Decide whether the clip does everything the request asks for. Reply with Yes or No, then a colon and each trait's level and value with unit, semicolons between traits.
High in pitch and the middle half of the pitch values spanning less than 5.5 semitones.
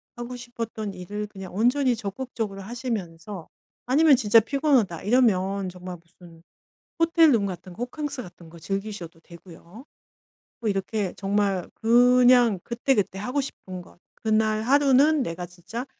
Yes: high, 215 Hz; average, 5.1 semitones